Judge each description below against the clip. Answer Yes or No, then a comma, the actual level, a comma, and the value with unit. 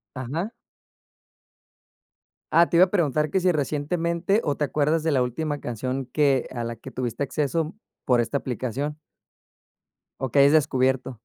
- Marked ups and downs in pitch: No, average, 3.7 semitones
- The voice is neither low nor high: Yes, medium, 145 Hz